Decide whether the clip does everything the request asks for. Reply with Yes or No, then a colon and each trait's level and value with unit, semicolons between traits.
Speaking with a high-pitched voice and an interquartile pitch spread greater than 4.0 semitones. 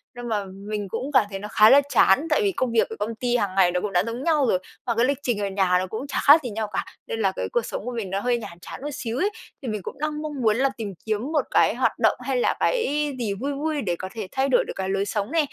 Yes: high, 230 Hz; wide, 5.4 semitones